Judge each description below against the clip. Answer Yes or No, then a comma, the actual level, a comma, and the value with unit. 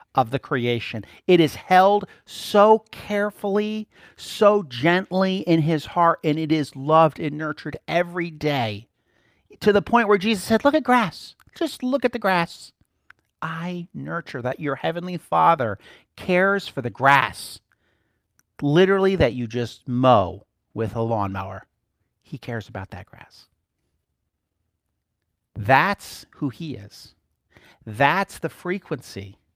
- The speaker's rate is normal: No, slow, 130 wpm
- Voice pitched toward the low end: No, medium, 155 Hz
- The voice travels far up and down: Yes, wide, 8.2 semitones